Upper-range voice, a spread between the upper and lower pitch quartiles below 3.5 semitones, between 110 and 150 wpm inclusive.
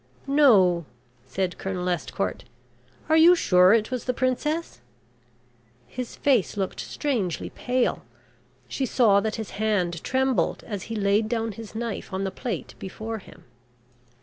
No: high, 220 Hz; average, 4.9 semitones; average, 140 wpm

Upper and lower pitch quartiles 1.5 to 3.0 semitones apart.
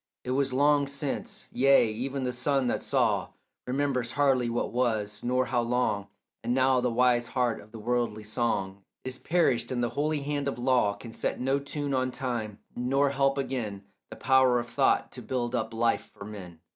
Yes: narrow, 2.5 semitones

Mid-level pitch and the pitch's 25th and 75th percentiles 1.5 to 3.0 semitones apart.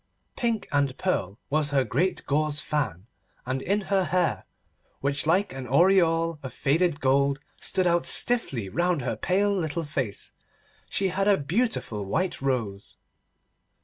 No: medium, 155 Hz; wide, 5.6 semitones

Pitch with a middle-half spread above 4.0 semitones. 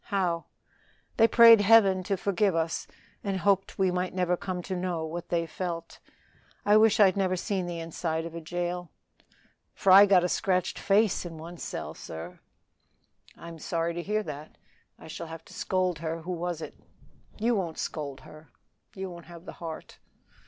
No: narrow, 2.6 semitones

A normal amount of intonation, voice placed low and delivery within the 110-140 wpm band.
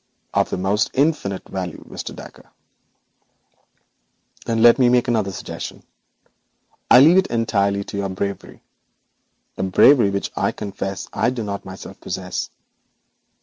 Yes: average, 3.6 semitones; low, 100 Hz; slow, 135 wpm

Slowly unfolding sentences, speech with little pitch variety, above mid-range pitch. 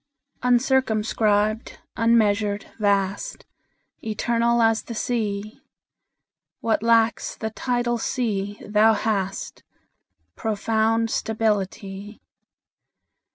Yes: slow, 70 wpm; narrow, 1.9 semitones; high, 220 Hz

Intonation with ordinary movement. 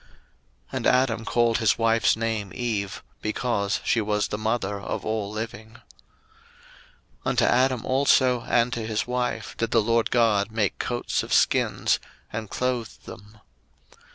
No: narrow, 2.2 semitones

